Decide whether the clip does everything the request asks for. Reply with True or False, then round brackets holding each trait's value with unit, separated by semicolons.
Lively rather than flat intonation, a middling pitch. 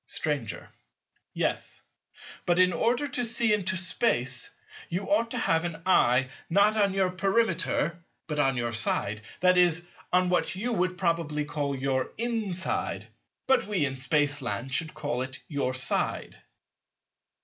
True (5.9 semitones; 170 Hz)